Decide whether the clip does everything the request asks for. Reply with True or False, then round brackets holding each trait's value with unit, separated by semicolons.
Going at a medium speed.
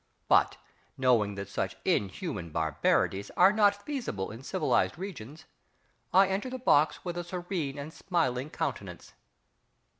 False (130 wpm)